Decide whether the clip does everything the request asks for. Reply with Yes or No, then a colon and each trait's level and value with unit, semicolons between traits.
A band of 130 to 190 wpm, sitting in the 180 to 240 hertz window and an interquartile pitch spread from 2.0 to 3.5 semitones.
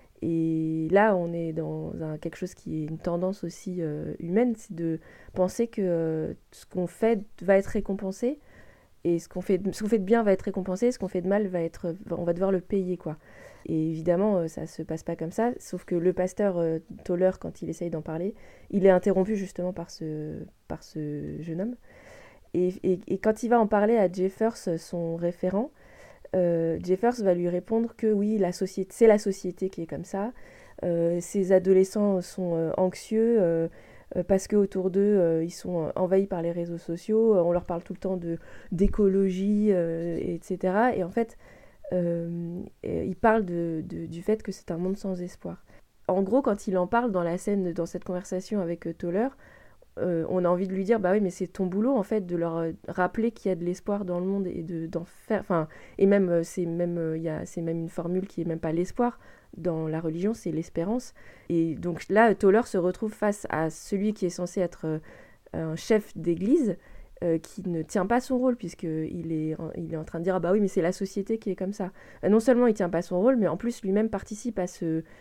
No: fast, 220 wpm; medium, 185 Hz; average, 3.1 semitones